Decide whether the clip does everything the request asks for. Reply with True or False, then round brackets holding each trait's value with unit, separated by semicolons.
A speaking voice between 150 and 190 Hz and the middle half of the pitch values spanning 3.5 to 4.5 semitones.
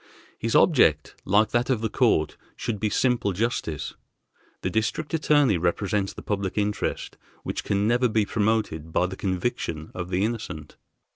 False (105 Hz; 4.2 semitones)